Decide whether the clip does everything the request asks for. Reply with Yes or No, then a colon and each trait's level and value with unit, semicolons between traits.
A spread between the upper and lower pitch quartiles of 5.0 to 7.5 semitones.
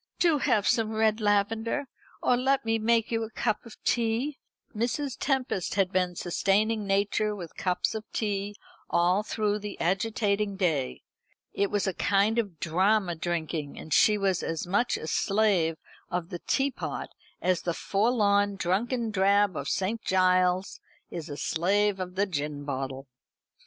No: average, 3.5 semitones